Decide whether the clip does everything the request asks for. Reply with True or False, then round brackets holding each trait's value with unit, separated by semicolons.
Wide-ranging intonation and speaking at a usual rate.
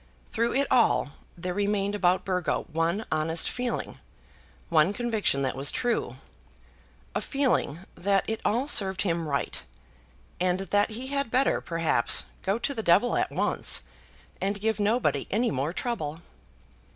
True (5.7 semitones; 145 wpm)